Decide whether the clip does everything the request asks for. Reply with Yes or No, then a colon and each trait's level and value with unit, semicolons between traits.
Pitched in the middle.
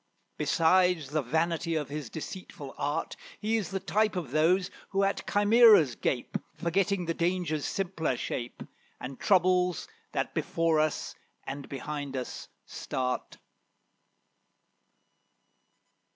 Yes: medium, 165 Hz